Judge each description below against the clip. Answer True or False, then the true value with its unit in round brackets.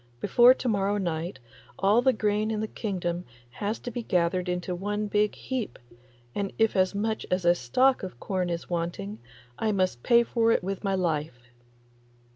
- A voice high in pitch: True (195 Hz)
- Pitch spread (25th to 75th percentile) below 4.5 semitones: True (3.8 semitones)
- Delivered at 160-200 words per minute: True (180 wpm)